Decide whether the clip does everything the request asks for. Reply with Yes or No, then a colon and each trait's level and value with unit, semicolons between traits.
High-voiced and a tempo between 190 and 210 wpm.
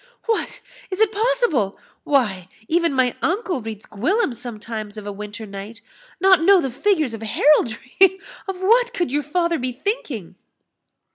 No: very high, 275 Hz; average, 150 wpm